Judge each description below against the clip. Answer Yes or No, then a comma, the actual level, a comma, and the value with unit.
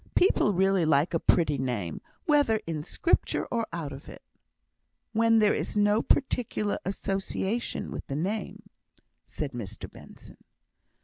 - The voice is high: Yes, high, 195 Hz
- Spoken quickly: No, slow, 135 wpm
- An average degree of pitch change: No, wide, 6.8 semitones